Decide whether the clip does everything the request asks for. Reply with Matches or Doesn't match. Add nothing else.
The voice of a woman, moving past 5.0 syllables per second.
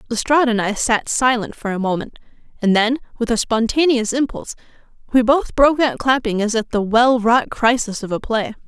Matches